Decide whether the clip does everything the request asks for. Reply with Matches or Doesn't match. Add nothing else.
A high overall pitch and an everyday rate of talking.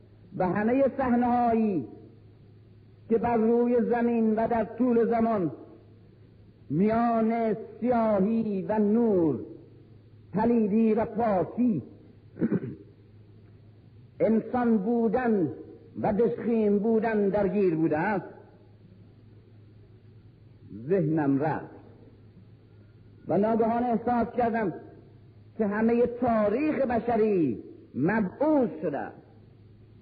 Doesn't match